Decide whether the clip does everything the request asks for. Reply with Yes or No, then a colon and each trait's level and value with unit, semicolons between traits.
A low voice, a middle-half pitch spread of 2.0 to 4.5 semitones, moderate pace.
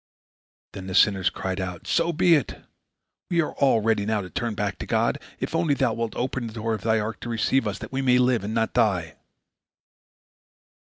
No: low, 115 Hz; average, 4.2 semitones; fast, 210 wpm